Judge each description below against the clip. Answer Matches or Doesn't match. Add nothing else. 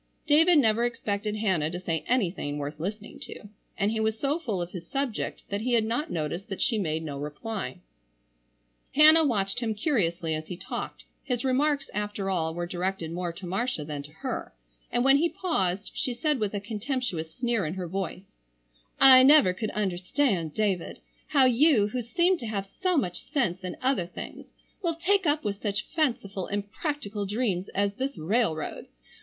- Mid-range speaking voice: Doesn't match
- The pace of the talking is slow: Doesn't match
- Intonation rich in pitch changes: Matches